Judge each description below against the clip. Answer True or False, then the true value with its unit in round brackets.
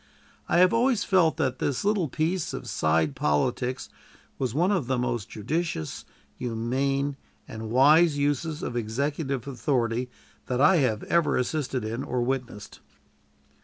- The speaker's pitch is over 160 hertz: False (135 Hz)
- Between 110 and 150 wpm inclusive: True (140 wpm)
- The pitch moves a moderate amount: True (4.8 semitones)